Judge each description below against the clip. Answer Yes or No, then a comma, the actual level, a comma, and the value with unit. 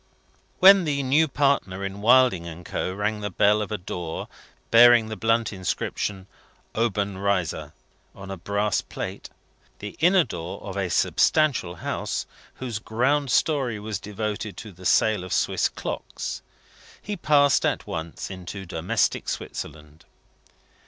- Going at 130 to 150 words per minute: Yes, average, 140 wpm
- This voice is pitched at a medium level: No, low, 105 Hz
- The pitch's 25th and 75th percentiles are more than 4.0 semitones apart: Yes, average, 5.0 semitones